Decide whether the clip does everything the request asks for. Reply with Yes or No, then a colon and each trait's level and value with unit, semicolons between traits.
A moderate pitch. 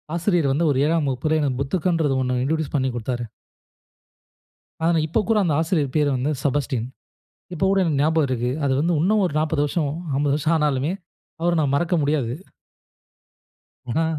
Yes: medium, 150 Hz